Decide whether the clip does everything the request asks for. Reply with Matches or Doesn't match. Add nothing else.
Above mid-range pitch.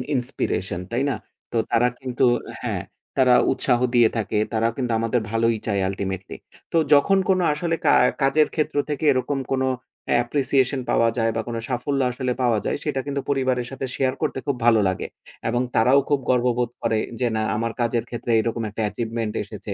Doesn't match